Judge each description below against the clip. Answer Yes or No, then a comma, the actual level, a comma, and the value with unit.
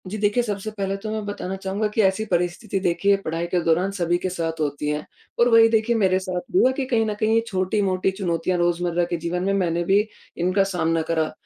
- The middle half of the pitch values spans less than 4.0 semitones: Yes, average, 3.3 semitones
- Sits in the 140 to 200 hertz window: Yes, high, 190 Hz